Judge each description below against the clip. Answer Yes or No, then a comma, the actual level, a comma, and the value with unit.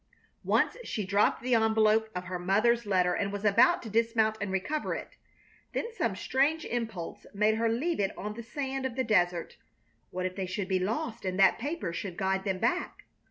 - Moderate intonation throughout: Yes, average, 3.8 semitones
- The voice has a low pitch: No, high, 215 Hz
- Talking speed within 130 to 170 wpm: No, average, 200 wpm